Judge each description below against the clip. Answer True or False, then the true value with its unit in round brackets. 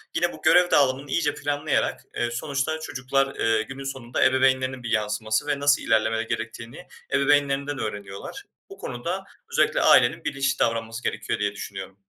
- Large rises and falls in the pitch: False (4.1 semitones)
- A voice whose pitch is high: False (130 Hz)